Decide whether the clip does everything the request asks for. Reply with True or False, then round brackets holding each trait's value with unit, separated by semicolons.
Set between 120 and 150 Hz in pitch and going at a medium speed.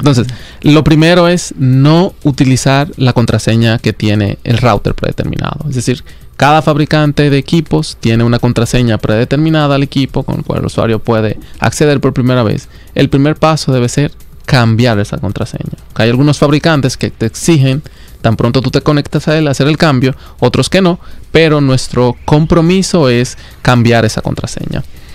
True (135 Hz; 165 wpm)